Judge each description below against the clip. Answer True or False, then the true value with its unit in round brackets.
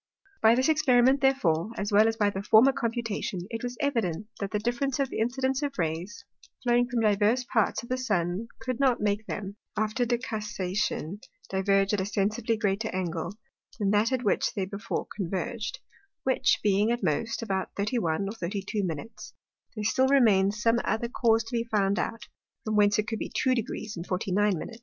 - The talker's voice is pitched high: True (215 Hz)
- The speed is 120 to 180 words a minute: False (190 wpm)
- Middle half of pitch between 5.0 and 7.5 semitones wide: False (3.3 semitones)